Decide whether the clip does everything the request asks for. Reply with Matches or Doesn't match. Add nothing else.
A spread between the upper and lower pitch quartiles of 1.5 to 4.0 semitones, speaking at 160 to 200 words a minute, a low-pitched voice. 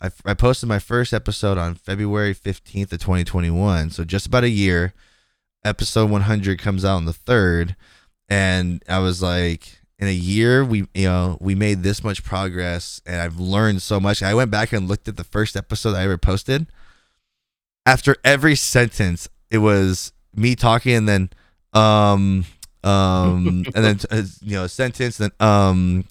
Matches